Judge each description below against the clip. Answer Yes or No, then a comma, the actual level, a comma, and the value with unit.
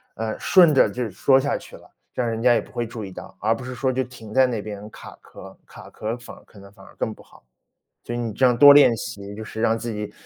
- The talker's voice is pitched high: No, low, 115 Hz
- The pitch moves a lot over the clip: No, average, 2.8 semitones